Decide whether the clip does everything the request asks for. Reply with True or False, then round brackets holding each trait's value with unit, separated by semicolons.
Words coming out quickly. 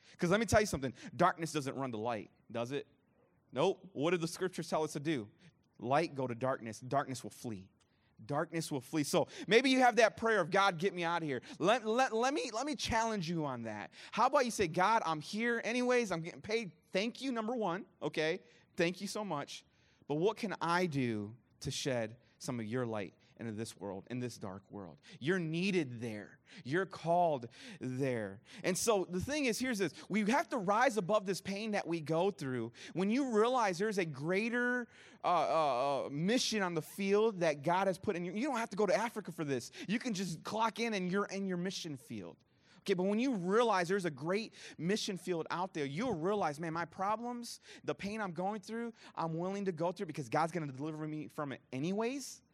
True (215 wpm)